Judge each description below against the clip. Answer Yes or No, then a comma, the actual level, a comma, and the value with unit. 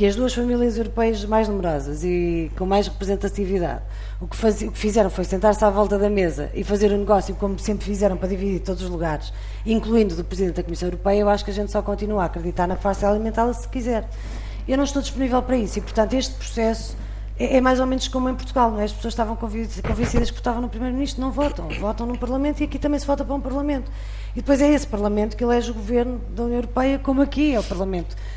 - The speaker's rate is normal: No, fast, 240 wpm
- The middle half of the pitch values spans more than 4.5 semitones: No, average, 4.2 semitones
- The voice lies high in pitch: Yes, high, 215 Hz